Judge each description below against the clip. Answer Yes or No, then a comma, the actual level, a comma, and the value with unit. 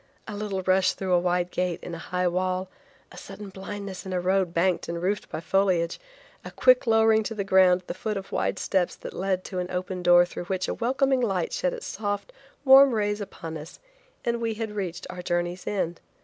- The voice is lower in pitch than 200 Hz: Yes, high, 190 Hz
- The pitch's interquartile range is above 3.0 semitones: No, average, 2.7 semitones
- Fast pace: Yes, fast, 220 wpm